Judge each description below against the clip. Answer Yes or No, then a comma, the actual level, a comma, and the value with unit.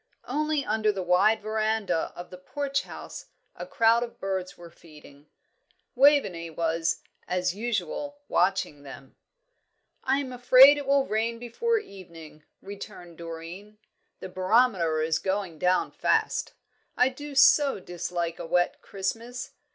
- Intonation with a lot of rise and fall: Yes, wide, 6.4 semitones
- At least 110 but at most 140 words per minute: Yes, slow, 135 wpm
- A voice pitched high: Yes, high, 200 Hz